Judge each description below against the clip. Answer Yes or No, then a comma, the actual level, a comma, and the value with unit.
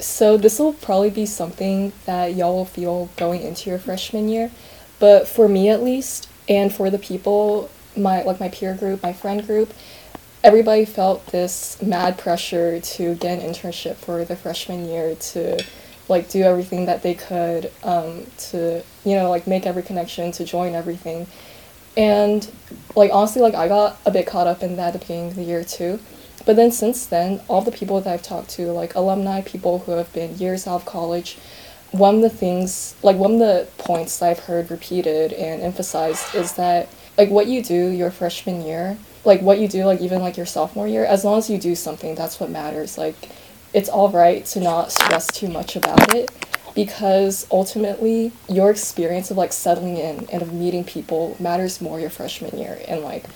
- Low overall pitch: No, medium, 185 Hz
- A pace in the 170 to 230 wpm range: Yes, average, 195 wpm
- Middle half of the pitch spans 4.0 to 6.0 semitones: No, average, 2.8 semitones